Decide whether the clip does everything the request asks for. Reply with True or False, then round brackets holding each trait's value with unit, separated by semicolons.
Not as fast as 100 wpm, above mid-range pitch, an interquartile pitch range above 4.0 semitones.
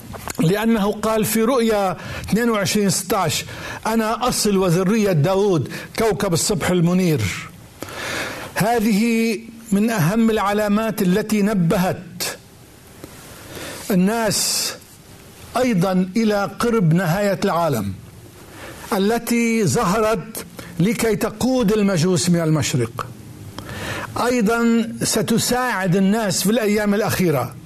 True (80 wpm; 200 Hz; 4.8 semitones)